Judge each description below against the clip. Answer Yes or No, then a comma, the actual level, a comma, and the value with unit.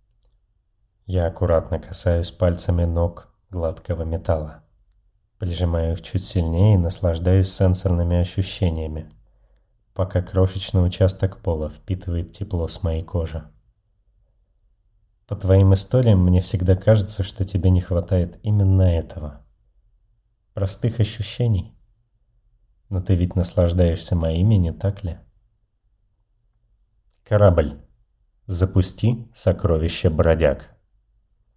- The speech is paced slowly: Yes, slow, 95 wpm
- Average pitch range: Yes, average, 3.2 semitones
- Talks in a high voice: No, very low, 95 Hz